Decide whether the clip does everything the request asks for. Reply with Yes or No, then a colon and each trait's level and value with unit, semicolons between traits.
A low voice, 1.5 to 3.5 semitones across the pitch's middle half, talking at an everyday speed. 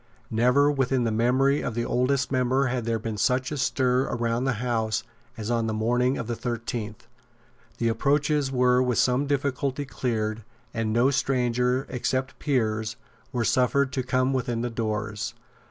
Yes: low, 125 Hz; narrow, 2.4 semitones; average, 165 wpm